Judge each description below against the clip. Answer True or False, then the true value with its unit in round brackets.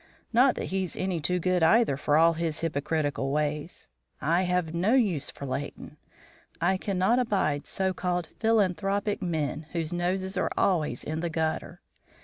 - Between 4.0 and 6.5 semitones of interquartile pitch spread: False (3.4 semitones)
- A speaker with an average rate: True (155 wpm)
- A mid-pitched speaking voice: True (175 Hz)